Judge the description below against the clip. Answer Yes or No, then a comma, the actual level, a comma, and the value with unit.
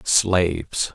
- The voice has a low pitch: Yes, very low, 85 Hz